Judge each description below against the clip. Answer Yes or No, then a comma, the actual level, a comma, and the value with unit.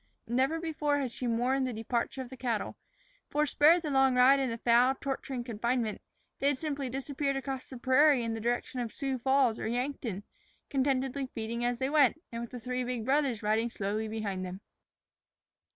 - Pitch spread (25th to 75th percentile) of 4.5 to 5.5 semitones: No, average, 2.7 semitones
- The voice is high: Yes, very high, 255 Hz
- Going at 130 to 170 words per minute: No, average, 185 wpm